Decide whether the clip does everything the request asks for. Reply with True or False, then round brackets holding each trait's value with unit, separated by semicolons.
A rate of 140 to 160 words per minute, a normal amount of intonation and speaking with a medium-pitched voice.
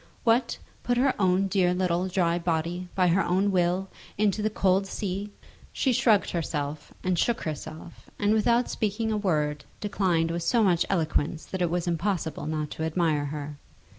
False (170 wpm; 3.7 semitones; 180 Hz)